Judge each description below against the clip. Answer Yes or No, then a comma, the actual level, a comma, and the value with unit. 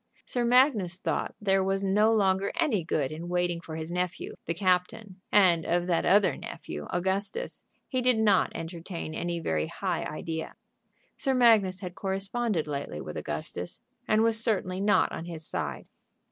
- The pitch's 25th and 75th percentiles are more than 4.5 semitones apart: No, average, 3.7 semitones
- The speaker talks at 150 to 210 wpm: Yes, average, 160 wpm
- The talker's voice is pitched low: No, medium, 185 Hz